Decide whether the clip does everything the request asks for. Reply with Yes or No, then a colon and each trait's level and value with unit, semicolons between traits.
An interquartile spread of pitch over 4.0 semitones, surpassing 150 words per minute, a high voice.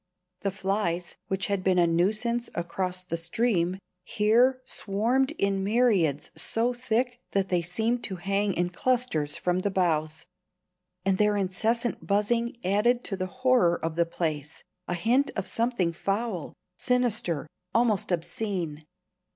No: average, 5.0 semitones; average, 140 wpm; high, 195 Hz